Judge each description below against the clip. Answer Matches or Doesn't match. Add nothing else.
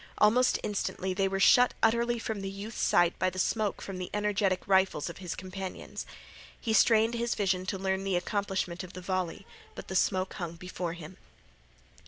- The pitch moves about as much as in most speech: Doesn't match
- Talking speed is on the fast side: Doesn't match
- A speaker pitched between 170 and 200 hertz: Matches